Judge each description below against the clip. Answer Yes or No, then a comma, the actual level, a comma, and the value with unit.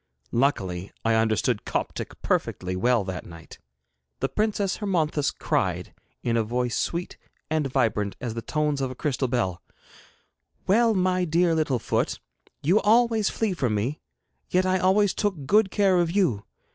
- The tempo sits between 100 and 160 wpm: Yes, average, 155 wpm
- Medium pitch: Yes, medium, 150 Hz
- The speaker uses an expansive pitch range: Yes, wide, 8.3 semitones